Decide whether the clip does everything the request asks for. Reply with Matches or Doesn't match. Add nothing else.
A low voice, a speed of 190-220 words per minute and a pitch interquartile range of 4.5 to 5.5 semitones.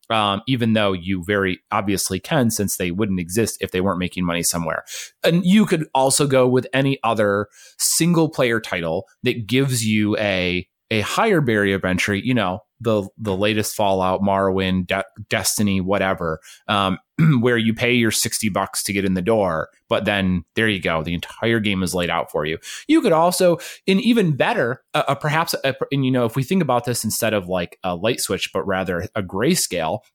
Matches